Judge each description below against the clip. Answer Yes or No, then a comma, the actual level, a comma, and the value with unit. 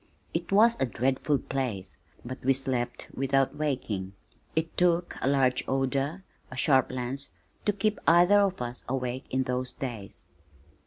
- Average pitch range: Yes, average, 4.1 semitones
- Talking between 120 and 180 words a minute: Yes, average, 150 wpm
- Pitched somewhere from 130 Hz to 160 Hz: Yes, low, 135 Hz